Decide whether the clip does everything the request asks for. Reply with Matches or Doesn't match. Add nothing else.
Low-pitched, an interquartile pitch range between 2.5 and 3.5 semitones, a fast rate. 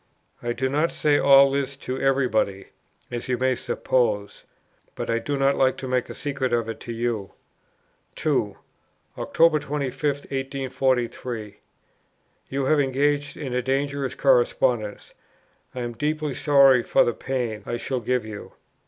Doesn't match